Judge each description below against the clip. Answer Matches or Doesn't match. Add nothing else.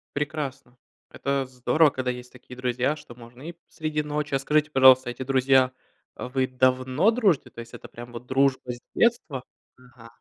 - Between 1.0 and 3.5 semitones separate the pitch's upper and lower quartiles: Matches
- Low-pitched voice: Matches